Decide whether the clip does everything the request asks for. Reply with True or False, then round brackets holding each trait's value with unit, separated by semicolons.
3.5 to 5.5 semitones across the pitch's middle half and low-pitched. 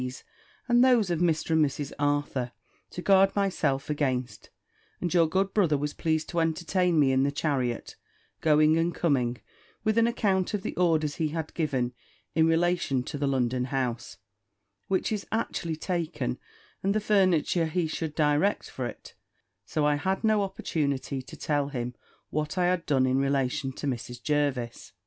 False (4.7 semitones; 155 Hz)